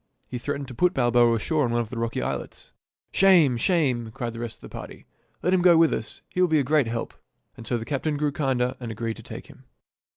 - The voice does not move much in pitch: No, average, 4.8 semitones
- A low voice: Yes, low, 130 Hz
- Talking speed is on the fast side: Yes, fast, 265 wpm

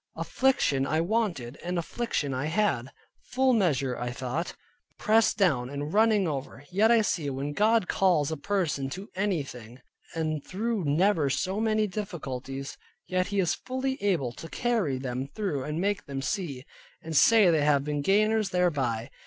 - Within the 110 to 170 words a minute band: Yes, average, 160 wpm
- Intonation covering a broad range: Yes, wide, 6.9 semitones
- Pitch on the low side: No, medium, 170 Hz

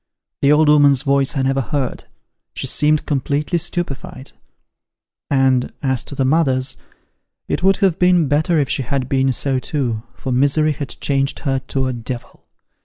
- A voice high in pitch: No, medium, 140 Hz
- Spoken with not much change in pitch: Yes, narrow, 2.3 semitones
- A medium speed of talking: Yes, average, 165 wpm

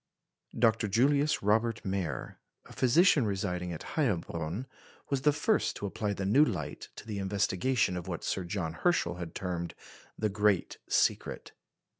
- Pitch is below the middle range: Yes, low, 100 Hz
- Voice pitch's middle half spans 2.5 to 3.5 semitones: No, average, 5.2 semitones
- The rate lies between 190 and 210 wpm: No, average, 150 wpm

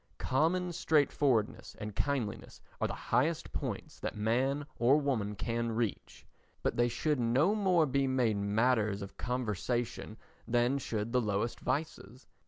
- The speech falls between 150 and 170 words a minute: No, average, 140 wpm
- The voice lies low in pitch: Yes, low, 120 Hz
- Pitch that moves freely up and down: No, average, 4.3 semitones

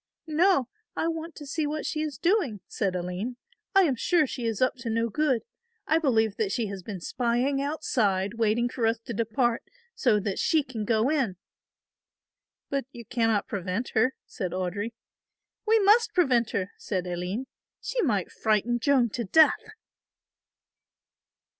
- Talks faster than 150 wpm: Yes, average, 160 wpm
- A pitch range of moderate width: No, wide, 6.0 semitones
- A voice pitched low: No, high, 240 Hz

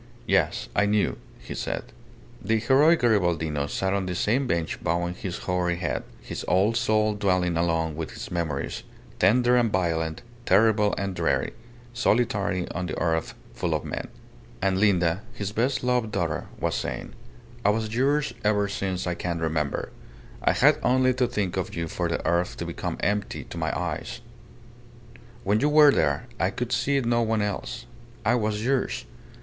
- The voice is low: Yes, low, 100 Hz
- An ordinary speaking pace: Yes, average, 170 wpm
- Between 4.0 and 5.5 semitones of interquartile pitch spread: Yes, average, 4.7 semitones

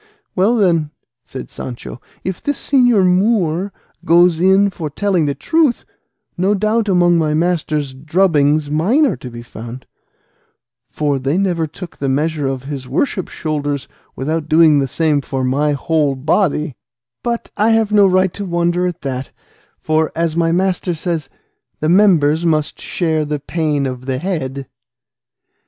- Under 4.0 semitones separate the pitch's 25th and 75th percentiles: No, average, 4.5 semitones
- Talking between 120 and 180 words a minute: Yes, average, 155 wpm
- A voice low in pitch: No, medium, 160 Hz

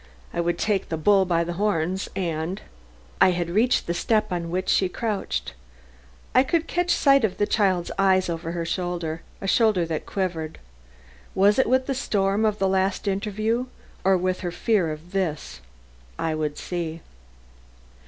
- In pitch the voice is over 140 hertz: Yes, medium, 185 Hz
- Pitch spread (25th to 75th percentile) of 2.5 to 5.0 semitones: Yes, average, 3.6 semitones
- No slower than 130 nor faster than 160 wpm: No, average, 170 wpm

